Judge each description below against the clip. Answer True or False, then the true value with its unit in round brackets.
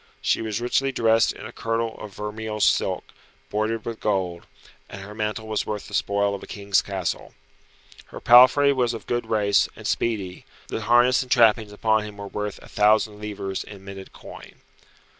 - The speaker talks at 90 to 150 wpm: False (180 wpm)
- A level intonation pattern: True (2.0 semitones)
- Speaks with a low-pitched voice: True (105 Hz)